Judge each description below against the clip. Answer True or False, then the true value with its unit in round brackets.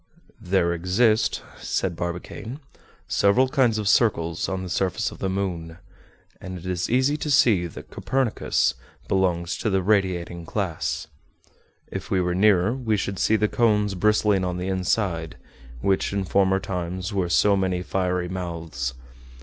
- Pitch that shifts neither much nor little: True (3.1 semitones)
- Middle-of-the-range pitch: False (95 Hz)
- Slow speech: False (150 wpm)